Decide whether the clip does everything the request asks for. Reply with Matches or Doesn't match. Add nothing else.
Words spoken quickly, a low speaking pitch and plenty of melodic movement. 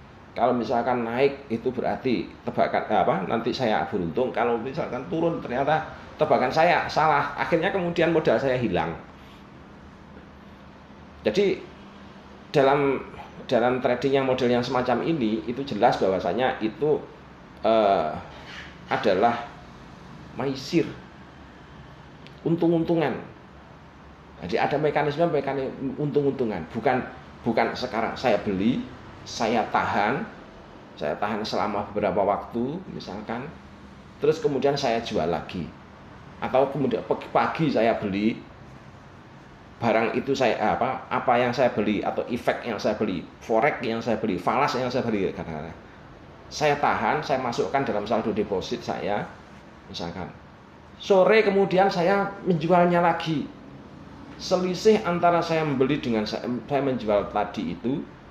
Doesn't match